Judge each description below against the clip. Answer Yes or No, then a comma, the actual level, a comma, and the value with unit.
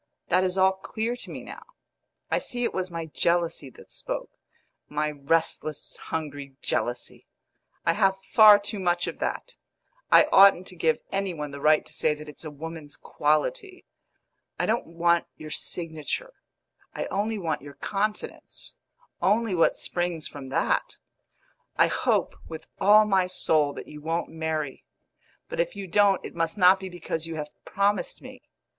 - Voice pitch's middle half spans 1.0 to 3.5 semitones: No, average, 4.1 semitones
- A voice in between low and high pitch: Yes, medium, 170 Hz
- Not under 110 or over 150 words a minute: No, average, 165 wpm